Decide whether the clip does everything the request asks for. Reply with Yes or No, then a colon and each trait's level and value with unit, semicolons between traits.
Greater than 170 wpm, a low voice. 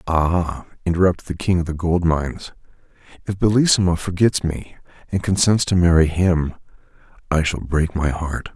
No: average, 155 wpm; very low, 85 Hz